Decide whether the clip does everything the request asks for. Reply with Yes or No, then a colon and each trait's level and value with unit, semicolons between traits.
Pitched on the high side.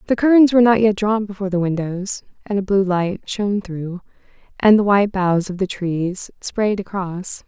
Yes: high, 195 Hz